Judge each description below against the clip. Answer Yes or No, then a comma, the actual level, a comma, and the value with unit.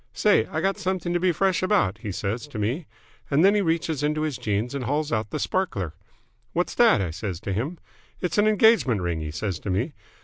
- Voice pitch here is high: No, medium, 145 Hz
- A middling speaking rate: No, fast, 225 wpm